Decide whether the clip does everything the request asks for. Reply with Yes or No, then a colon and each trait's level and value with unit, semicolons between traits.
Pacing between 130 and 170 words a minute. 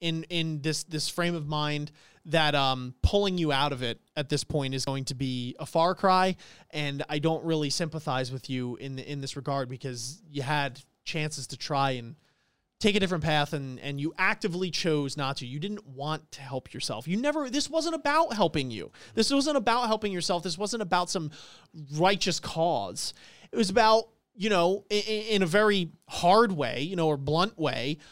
No: average, 200 wpm